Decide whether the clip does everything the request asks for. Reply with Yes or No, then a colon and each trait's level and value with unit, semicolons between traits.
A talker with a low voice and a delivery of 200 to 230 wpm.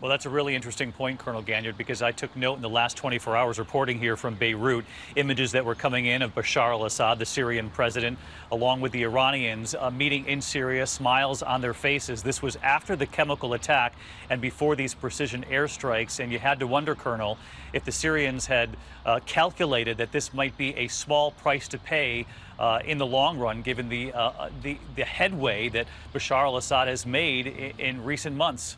Yes: low, 130 Hz; fast, 205 wpm